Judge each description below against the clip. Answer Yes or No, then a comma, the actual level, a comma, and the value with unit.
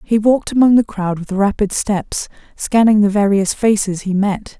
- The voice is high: Yes, high, 205 Hz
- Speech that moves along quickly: No, average, 185 wpm